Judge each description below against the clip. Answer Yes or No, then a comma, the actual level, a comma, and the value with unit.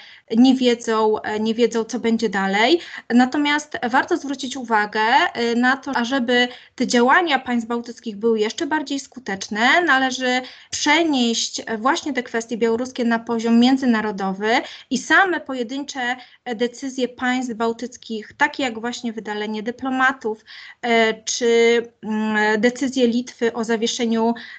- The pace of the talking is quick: No, average, 115 wpm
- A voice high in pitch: Yes, high, 240 Hz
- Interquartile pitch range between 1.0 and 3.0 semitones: Yes, narrow, 2.4 semitones